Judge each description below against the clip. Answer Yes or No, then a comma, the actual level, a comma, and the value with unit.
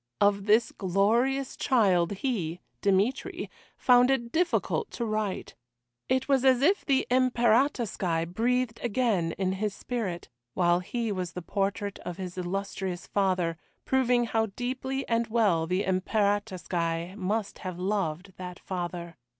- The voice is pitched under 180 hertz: No, high, 205 Hz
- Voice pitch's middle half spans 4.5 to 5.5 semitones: Yes, average, 4.9 semitones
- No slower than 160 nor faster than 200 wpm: No, slow, 135 wpm